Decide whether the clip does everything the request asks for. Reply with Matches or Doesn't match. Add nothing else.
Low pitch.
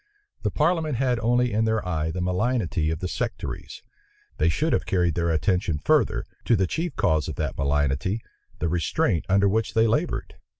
Matches